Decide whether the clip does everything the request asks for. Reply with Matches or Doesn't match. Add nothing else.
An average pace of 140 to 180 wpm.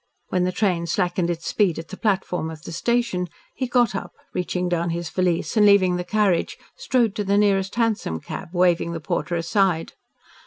Doesn't match